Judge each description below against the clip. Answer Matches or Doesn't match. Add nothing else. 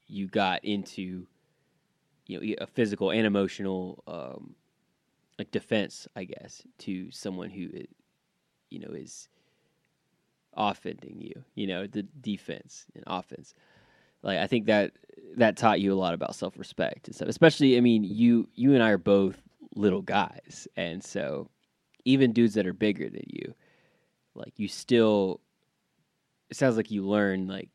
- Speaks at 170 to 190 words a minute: Doesn't match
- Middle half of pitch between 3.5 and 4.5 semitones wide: Doesn't match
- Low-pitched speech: Matches